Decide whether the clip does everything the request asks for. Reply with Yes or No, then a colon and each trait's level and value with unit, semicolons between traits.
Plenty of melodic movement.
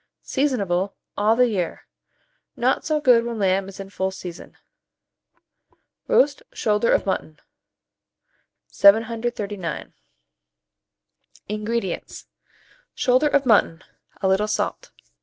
No: average, 3.8 semitones